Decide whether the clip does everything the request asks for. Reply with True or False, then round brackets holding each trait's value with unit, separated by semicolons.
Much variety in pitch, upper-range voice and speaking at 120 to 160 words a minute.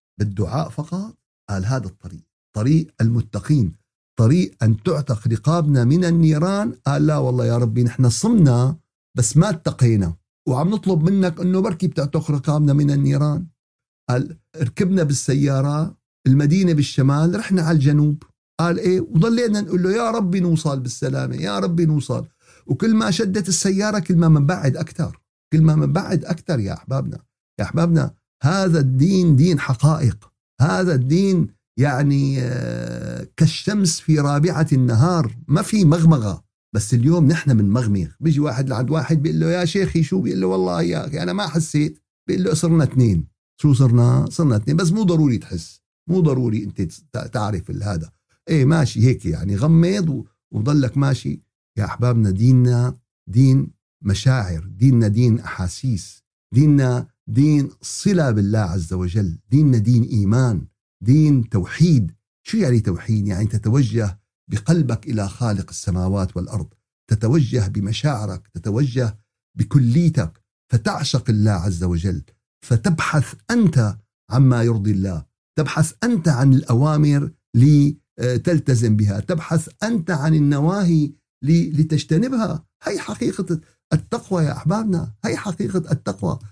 False (6.4 semitones; 140 Hz; 130 wpm)